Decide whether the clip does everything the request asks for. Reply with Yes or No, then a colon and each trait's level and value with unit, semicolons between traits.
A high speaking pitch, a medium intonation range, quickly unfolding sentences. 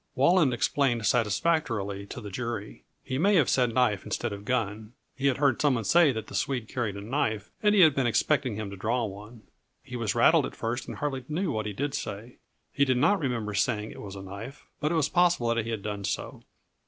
No: low, 120 Hz; average, 4.9 semitones; fast, 230 wpm